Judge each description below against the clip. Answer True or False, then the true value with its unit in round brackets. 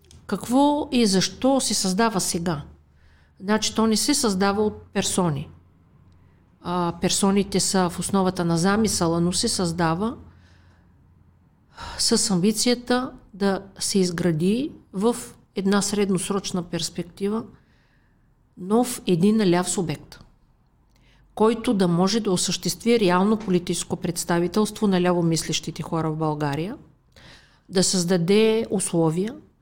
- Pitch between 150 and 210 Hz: True (185 Hz)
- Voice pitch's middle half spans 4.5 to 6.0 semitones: False (3.9 semitones)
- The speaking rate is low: True (105 wpm)